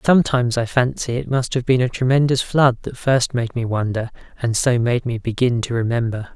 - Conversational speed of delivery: No, fast, 210 wpm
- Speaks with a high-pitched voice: No, low, 125 Hz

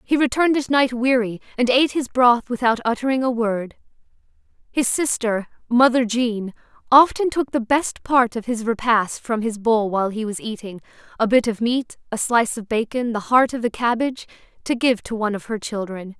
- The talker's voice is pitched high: Yes, high, 235 Hz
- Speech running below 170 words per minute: No, average, 185 wpm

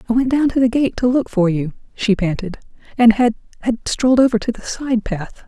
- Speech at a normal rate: No, fast, 220 wpm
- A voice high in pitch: Yes, high, 230 Hz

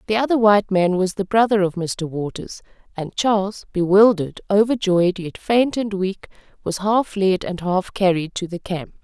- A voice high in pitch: Yes, high, 195 Hz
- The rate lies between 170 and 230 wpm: Yes, average, 180 wpm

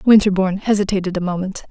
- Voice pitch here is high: Yes, high, 195 Hz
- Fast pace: No, average, 140 wpm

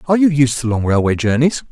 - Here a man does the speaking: Yes, male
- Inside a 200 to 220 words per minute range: No, fast, 245 wpm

